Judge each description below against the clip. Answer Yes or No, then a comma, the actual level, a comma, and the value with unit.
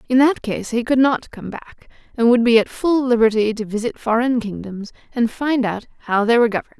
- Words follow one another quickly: Yes, fast, 220 wpm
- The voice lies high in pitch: Yes, high, 235 Hz